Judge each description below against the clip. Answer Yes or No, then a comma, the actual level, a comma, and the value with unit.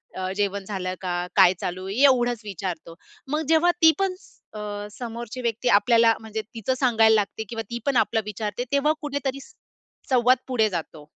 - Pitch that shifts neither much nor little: Yes, average, 4.1 semitones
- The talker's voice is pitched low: No, high, 225 Hz